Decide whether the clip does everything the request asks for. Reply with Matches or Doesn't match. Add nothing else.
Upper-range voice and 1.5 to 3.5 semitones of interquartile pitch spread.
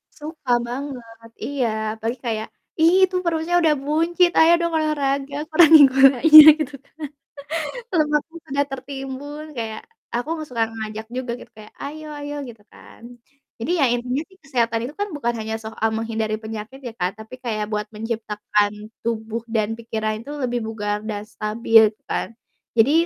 Doesn't match